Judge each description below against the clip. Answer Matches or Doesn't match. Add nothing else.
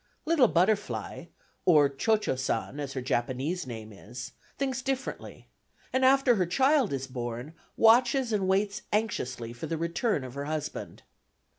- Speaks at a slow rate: Doesn't match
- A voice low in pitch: Doesn't match